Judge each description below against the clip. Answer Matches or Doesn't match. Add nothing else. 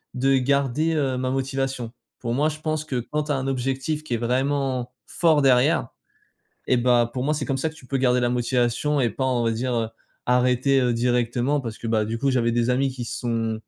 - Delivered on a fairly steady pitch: Matches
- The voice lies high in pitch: Doesn't match